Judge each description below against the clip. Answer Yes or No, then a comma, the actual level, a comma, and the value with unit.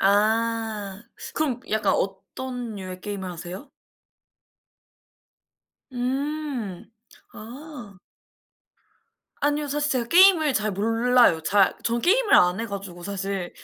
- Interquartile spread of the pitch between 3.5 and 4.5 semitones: No, average, 5.3 semitones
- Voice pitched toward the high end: Yes, high, 225 Hz